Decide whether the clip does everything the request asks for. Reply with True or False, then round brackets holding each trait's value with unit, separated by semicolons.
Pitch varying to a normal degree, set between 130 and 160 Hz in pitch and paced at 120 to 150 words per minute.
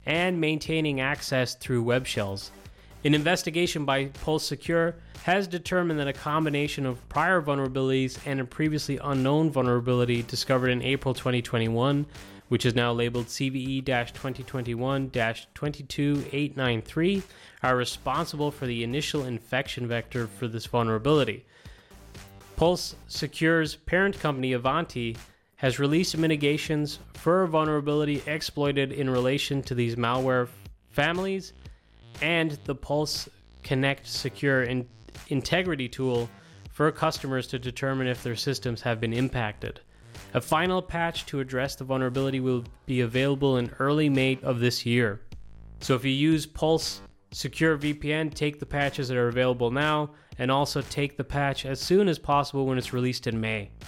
True (3.4 semitones; 135 Hz; 140 wpm)